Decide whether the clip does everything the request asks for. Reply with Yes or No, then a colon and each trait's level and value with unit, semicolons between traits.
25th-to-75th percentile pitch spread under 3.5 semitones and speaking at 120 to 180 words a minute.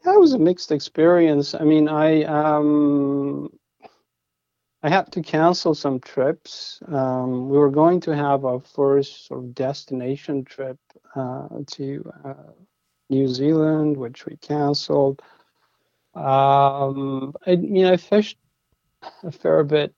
Yes: average, 2.8 semitones; average, 140 wpm